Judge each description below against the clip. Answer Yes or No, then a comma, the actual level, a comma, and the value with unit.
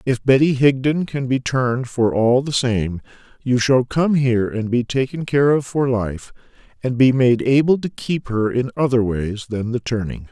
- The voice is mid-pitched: No, low, 125 Hz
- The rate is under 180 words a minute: No, average, 200 wpm